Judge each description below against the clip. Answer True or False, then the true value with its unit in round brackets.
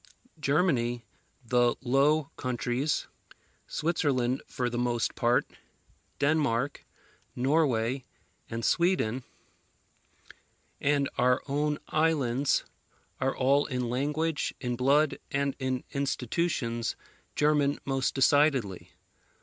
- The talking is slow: True (90 wpm)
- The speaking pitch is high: False (135 Hz)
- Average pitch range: True (3.1 semitones)